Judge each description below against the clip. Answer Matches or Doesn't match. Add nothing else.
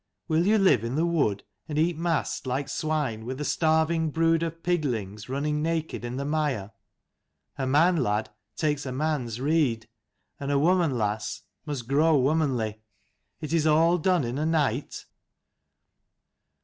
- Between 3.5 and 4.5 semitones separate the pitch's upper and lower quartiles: Matches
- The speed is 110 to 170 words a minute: Matches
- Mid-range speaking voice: Matches